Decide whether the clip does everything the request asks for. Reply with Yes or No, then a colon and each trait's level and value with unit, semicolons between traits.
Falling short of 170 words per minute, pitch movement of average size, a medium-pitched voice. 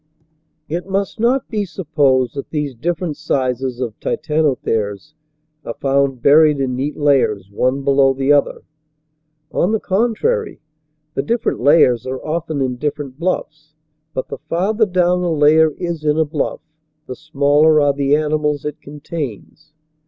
Yes: average, 145 wpm; average, 3.6 semitones; medium, 150 Hz